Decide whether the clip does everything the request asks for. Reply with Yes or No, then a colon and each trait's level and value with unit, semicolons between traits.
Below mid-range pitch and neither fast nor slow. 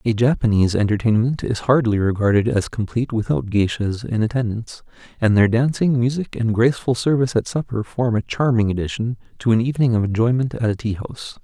Yes: low, 115 Hz; average, 180 wpm